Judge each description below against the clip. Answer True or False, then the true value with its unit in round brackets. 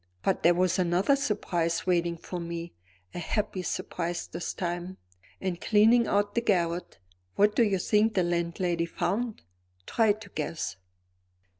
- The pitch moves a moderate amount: True (3.4 semitones)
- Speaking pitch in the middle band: True (180 Hz)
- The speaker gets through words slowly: False (145 wpm)